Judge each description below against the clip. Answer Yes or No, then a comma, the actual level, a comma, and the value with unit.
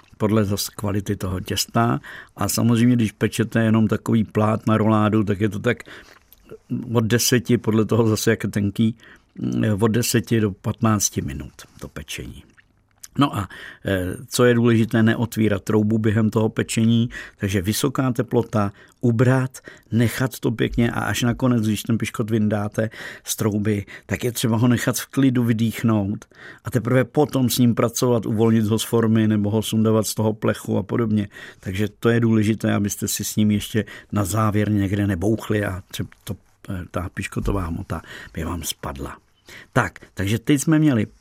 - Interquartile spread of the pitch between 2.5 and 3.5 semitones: No, narrow, 2.1 semitones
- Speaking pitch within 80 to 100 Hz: No, low, 110 Hz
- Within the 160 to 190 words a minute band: Yes, average, 165 wpm